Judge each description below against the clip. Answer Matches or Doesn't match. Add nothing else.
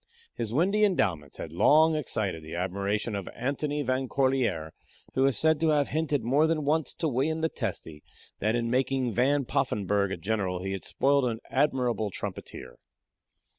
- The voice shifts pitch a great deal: Matches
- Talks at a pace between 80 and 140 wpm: Doesn't match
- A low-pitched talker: Matches